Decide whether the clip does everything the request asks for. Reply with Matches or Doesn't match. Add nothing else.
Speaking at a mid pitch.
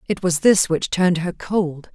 Matches